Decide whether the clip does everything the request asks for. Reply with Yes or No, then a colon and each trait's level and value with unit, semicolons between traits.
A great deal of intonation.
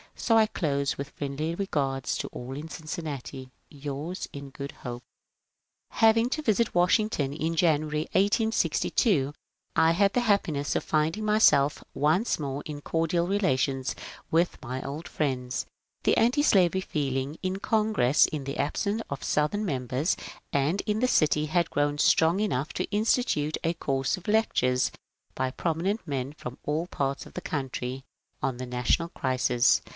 Yes: wide, 5.7 semitones